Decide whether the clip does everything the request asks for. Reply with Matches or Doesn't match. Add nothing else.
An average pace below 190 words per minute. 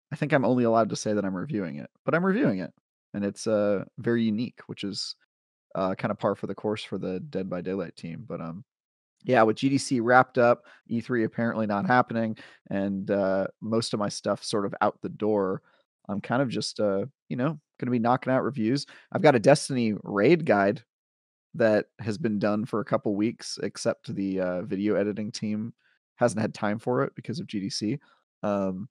Doesn't match